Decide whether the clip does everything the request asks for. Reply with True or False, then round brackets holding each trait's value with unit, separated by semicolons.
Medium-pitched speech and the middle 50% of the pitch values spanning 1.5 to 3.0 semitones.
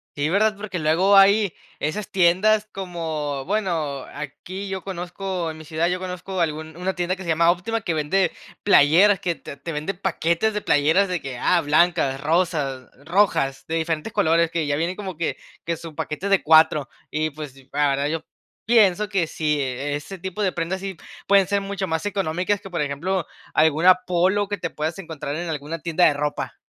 False (170 Hz; 3.9 semitones)